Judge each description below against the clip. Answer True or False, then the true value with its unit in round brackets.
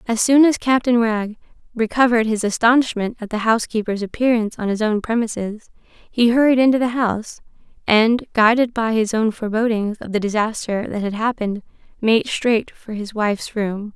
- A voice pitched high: True (225 Hz)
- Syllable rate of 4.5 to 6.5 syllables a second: True (5.4 syllables/s)